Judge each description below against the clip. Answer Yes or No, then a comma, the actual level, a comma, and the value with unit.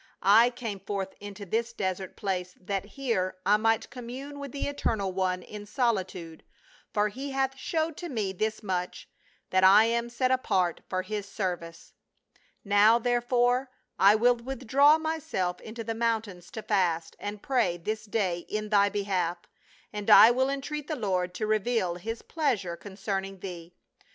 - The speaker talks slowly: No, average, 160 wpm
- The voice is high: Yes, high, 210 Hz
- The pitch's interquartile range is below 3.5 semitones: No, average, 4.3 semitones